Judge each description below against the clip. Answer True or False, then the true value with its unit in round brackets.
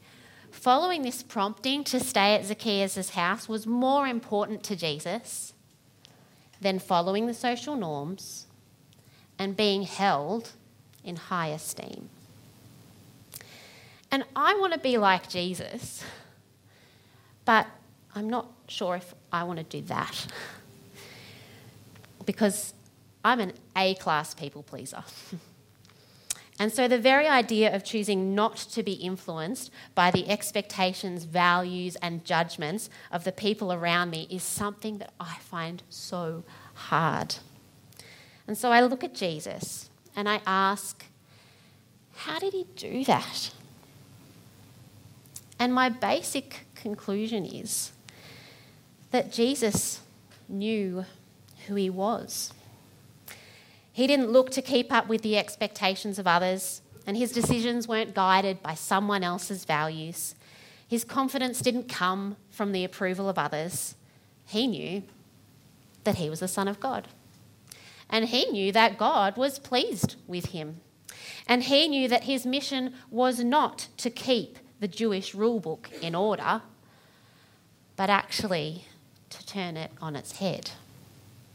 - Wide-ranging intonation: True (5.9 semitones)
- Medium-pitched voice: False (195 Hz)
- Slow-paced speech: True (125 wpm)